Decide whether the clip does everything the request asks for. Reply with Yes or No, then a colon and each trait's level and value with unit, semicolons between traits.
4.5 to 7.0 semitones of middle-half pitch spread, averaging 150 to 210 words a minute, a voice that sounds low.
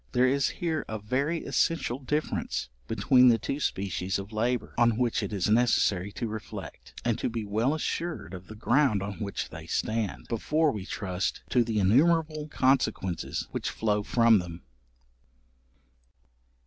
Yes: average, 5.0 semitones; average, 155 wpm; low, 115 Hz